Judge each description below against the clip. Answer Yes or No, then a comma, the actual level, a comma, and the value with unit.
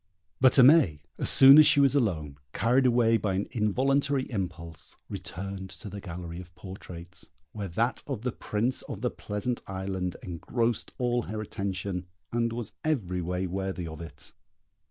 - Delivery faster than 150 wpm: Yes, average, 160 wpm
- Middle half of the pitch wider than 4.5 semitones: Yes, average, 5.1 semitones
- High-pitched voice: No, low, 100 Hz